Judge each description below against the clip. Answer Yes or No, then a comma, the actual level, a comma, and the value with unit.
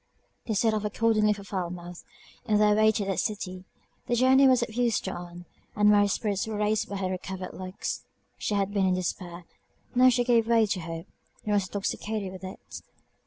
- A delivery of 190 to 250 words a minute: Yes, average, 200 wpm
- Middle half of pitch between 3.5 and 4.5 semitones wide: No, average, 2.8 semitones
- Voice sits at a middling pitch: No, high, 205 Hz